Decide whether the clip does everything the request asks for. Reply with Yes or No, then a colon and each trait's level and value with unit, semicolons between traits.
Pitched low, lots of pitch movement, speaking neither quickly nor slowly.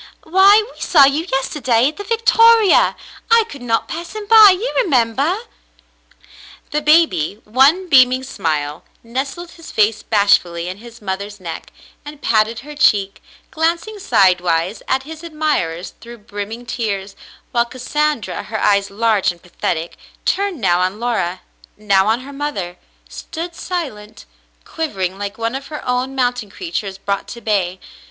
No: high, 240 Hz; wide, 7.7 semitones; average, 150 wpm